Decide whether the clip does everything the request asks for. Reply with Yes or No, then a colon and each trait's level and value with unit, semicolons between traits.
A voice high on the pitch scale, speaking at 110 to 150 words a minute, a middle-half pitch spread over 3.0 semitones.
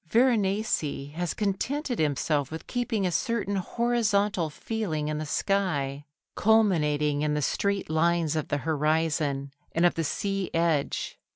No: medium, 170 Hz; slow, 135 wpm; average, 5.2 semitones